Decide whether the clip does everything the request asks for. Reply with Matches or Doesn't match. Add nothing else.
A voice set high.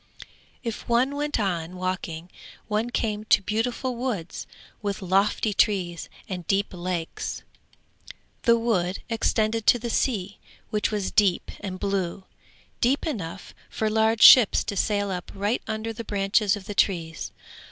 Matches